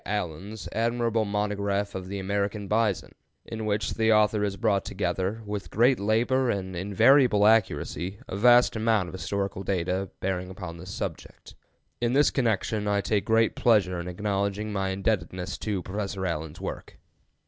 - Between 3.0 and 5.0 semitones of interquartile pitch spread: No, narrow, 2.6 semitones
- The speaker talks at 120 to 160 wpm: Yes, average, 155 wpm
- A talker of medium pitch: No, low, 100 Hz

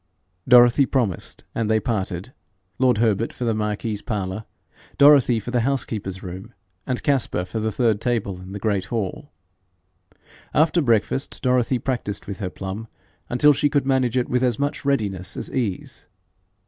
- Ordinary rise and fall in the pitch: Yes, average, 4.1 semitones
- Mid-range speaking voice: No, low, 115 Hz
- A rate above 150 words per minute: Yes, average, 160 wpm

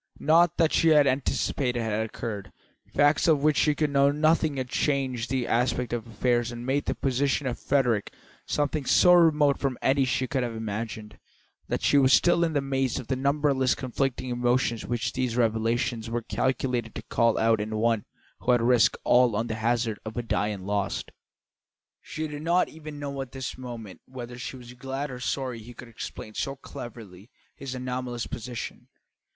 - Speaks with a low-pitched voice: Yes, low, 125 Hz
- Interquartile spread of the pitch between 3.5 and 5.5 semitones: No, average, 3.0 semitones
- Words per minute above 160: Yes, average, 185 wpm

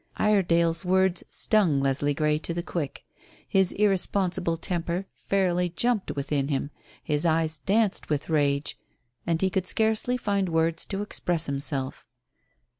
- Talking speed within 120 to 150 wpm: Yes, slow, 135 wpm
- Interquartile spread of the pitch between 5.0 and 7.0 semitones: No, average, 4.1 semitones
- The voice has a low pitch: No, medium, 170 Hz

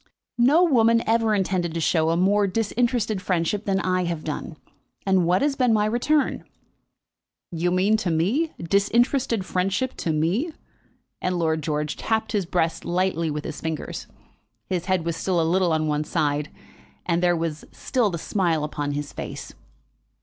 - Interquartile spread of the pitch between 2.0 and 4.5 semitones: No, average, 4.9 semitones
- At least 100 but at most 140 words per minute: No, average, 165 wpm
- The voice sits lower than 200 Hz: Yes, medium, 185 Hz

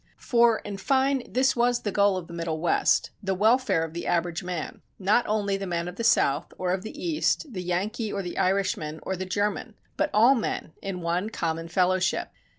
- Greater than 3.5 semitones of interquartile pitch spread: Yes, average, 4.3 semitones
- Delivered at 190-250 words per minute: Yes, fast, 205 wpm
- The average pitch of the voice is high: Yes, high, 195 Hz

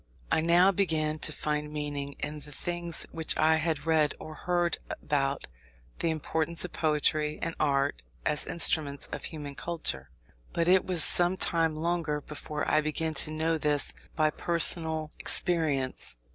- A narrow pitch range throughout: Yes, narrow, 2.0 semitones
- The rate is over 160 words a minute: No, average, 155 wpm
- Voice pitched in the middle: Yes, medium, 155 Hz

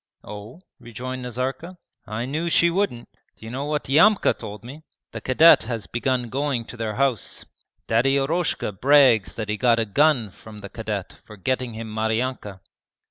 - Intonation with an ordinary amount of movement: Yes, average, 3.9 semitones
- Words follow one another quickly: No, average, 165 wpm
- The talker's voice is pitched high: No, low, 125 Hz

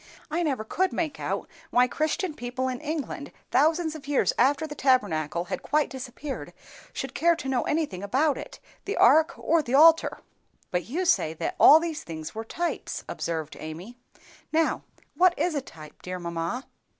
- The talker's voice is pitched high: Yes, very high, 275 Hz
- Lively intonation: Yes, wide, 6.7 semitones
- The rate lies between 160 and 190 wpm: Yes, average, 175 wpm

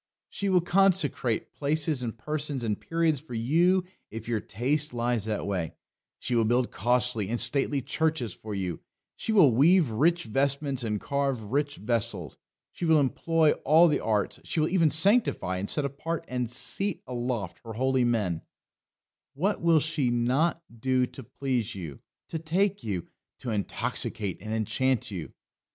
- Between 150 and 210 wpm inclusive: Yes, average, 160 wpm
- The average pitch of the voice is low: Yes, low, 130 Hz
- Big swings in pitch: Yes, wide, 5.8 semitones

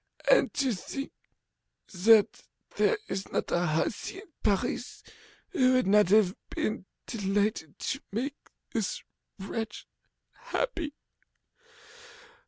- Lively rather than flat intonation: Yes, wide, 5.9 semitones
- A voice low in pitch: No, high, 220 Hz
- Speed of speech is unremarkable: No, slow, 105 wpm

